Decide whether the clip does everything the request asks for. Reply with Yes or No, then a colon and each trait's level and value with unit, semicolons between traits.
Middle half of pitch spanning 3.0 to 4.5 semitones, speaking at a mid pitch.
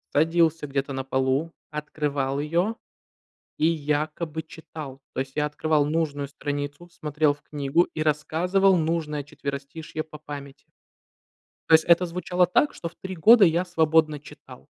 No: narrow, 2.4 semitones; medium, 155 Hz